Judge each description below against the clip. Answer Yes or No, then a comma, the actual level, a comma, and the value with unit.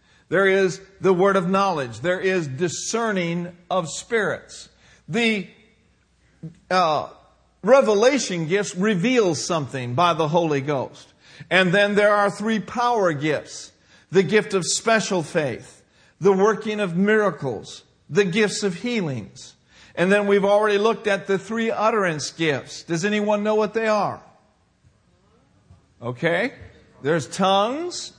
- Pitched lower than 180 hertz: No, high, 195 Hz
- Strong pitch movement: No, average, 3.7 semitones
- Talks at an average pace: No, slow, 130 wpm